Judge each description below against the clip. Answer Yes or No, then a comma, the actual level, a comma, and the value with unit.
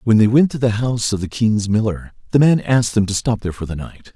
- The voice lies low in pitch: Yes, low, 115 Hz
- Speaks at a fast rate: Yes, fast, 290 wpm